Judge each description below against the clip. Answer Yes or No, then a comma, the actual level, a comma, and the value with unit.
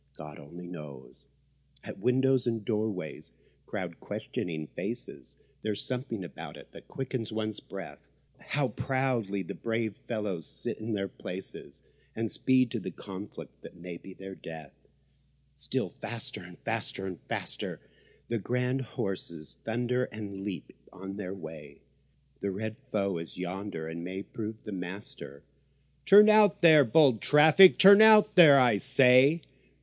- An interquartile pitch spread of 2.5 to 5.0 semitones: No, wide, 5.6 semitones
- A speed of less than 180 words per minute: Yes, average, 145 wpm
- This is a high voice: No, low, 105 Hz